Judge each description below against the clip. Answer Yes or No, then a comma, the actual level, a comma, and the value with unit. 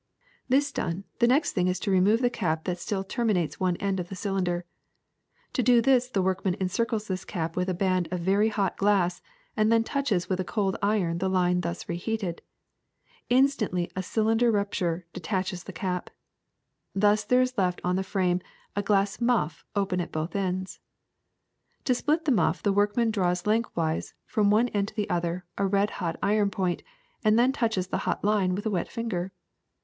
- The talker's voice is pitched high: Yes, high, 195 Hz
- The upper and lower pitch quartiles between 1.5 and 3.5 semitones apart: Yes, average, 3.2 semitones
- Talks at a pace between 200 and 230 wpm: No, average, 190 wpm